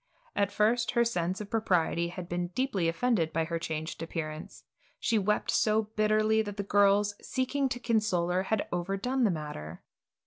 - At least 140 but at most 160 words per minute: No, average, 170 wpm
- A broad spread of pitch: No, average, 4.3 semitones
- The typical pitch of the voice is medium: No, high, 200 Hz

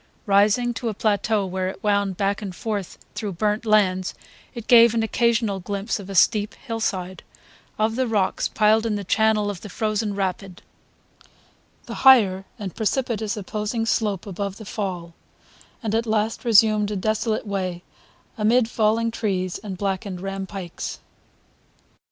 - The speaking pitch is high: Yes, high, 210 Hz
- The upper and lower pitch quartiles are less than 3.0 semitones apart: Yes, narrow, 2.4 semitones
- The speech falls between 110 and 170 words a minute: Yes, average, 150 wpm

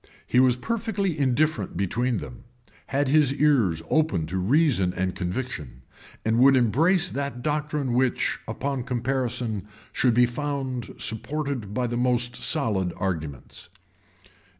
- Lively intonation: No, average, 5.0 semitones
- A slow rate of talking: Yes, slow, 125 wpm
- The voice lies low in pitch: Yes, low, 125 Hz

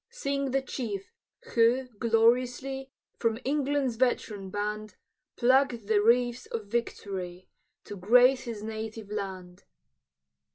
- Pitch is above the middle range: Yes, high, 230 Hz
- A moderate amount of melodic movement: Yes, average, 3.7 semitones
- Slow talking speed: Yes, slow, 110 wpm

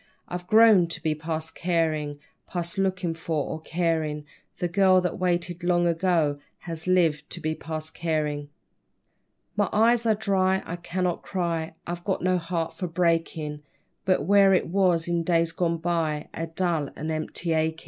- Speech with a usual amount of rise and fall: No, narrow, 2.2 semitones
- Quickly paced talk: No, average, 165 wpm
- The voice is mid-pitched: Yes, medium, 170 Hz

